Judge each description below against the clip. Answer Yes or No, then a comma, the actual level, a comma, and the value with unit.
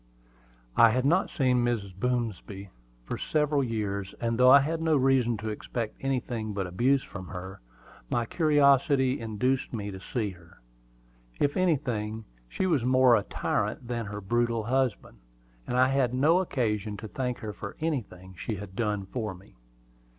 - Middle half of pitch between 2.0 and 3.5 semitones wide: No, average, 4.3 semitones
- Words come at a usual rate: Yes, average, 165 wpm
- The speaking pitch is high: No, low, 120 Hz